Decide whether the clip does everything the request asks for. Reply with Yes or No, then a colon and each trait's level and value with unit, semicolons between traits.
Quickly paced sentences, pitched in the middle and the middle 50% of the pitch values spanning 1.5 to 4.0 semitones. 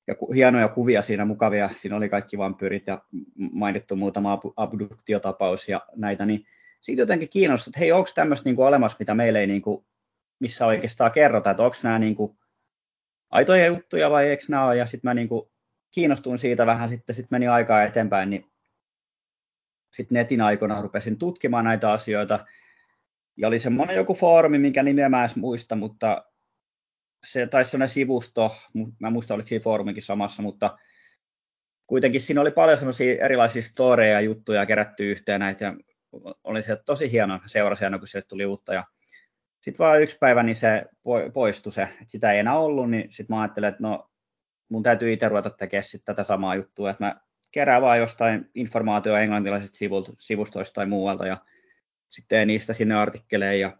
No: fast, 165 wpm; low, 110 Hz; average, 3.4 semitones